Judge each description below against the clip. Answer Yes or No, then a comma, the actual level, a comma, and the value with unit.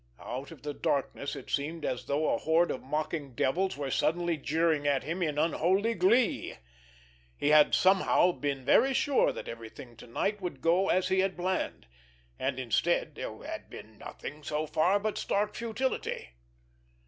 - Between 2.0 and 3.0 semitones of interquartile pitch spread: No, average, 4.8 semitones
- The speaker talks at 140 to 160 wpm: No, average, 170 wpm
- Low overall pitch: No, medium, 160 Hz